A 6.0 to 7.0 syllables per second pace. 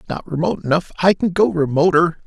Yes: 6.3 syllables/s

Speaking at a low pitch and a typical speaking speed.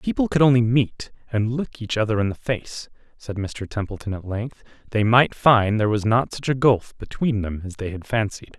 No: low, 110 Hz; fast, 225 wpm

